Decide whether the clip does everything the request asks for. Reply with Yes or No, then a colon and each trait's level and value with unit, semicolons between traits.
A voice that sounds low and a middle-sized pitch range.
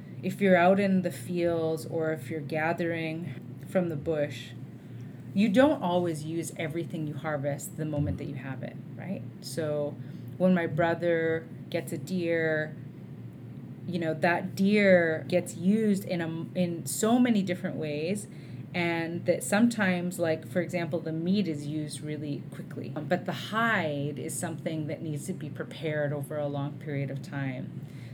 No: medium, 160 Hz; average, 3.3 semitones